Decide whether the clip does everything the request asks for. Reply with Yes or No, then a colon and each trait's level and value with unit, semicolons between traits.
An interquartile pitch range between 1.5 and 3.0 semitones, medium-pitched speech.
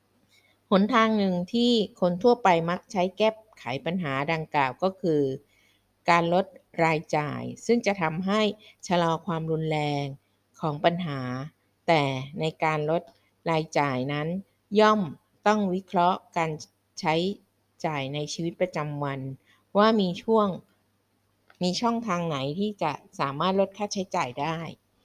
No: average, 5.2 semitones; medium, 165 Hz